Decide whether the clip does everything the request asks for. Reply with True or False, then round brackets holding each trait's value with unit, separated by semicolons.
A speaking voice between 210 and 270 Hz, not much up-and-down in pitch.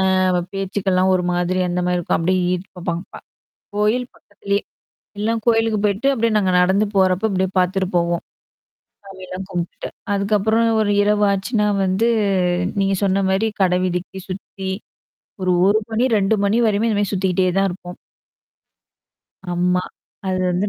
False (195 Hz; 2.3 semitones)